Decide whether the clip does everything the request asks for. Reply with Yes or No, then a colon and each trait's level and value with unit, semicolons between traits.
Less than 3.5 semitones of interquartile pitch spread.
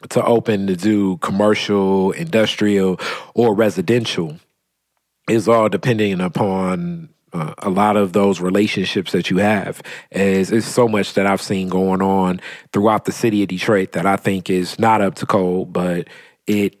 Yes: narrow, 2.6 semitones